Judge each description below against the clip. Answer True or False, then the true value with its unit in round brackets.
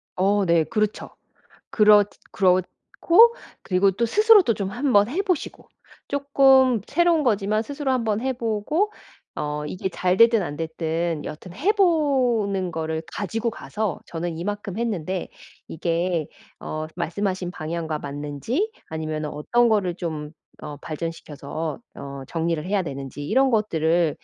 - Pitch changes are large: True (6.7 semitones)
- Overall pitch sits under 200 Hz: True (190 Hz)